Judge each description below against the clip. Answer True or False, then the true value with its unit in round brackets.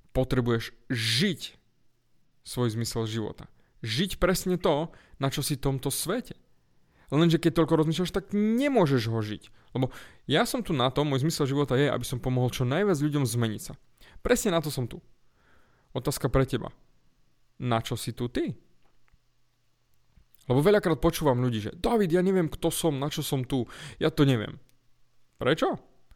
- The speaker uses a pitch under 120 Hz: False (135 Hz)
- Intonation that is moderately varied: True (4.9 semitones)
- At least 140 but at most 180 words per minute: True (165 wpm)